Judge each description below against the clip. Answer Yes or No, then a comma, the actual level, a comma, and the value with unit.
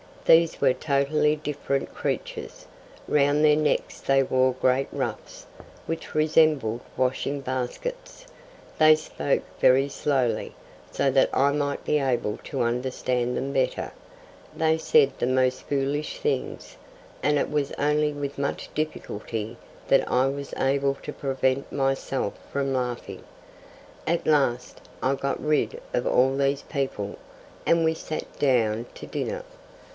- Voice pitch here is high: No, medium, 140 Hz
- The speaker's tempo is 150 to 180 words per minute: No, slow, 135 wpm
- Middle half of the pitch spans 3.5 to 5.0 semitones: No, narrow, 2.6 semitones